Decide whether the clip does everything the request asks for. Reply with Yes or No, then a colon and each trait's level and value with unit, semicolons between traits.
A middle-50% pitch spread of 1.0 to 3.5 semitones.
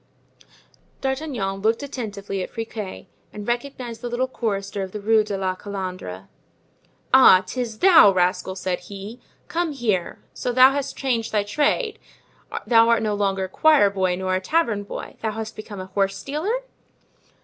No: average, 4.8 semitones